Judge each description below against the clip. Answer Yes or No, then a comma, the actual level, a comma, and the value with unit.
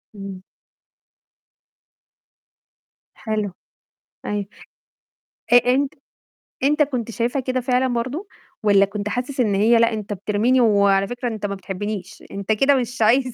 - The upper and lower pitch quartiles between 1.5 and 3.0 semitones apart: No, average, 3.8 semitones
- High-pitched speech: Yes, high, 225 Hz